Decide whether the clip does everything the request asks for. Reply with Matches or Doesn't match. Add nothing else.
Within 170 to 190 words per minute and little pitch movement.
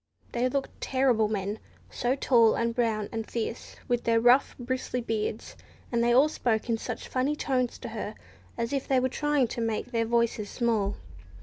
Matches